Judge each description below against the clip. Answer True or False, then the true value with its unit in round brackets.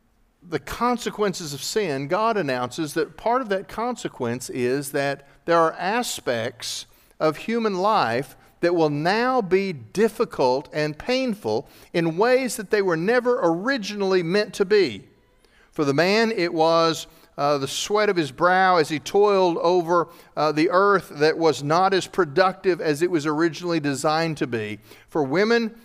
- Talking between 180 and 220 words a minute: False (160 wpm)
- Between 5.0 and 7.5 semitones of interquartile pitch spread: True (5.3 semitones)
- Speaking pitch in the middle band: True (170 Hz)